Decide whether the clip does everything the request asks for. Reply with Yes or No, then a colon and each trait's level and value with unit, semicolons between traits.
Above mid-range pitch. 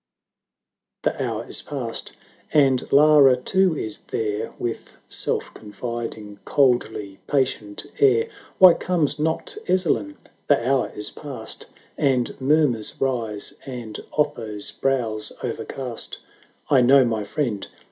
No: low, 125 Hz